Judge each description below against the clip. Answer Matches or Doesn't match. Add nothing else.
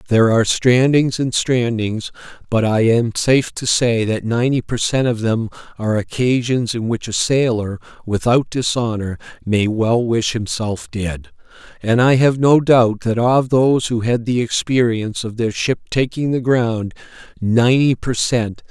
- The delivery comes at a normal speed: Matches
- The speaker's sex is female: Doesn't match